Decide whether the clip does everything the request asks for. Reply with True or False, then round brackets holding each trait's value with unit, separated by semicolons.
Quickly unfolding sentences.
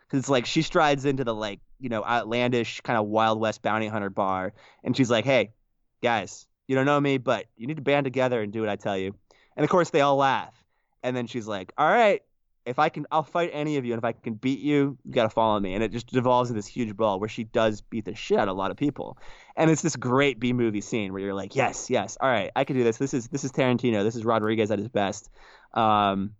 True (275 wpm)